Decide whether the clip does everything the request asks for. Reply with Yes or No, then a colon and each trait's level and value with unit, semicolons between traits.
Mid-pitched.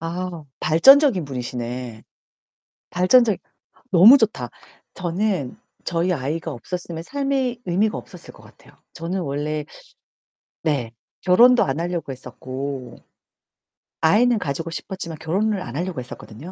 Yes: medium, 170 Hz